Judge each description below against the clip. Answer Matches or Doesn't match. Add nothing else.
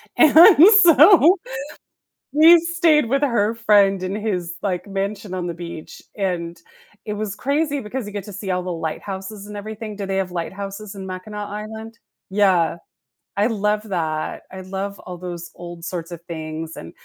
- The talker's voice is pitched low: Doesn't match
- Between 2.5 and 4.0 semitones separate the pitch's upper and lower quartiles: Matches